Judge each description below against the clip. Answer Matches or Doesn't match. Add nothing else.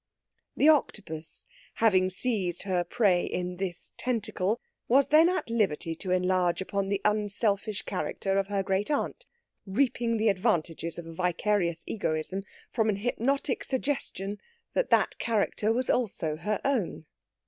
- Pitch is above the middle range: Matches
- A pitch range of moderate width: Matches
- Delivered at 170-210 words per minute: Doesn't match